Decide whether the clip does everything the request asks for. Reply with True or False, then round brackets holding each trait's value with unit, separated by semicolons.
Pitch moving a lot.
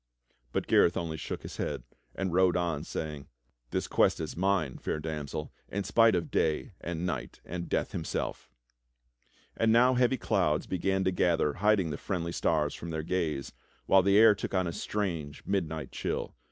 False (3.7 semitones)